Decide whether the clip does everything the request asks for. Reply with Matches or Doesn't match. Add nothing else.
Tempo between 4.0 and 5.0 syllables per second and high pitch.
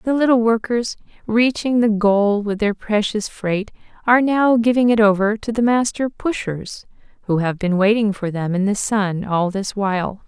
Matches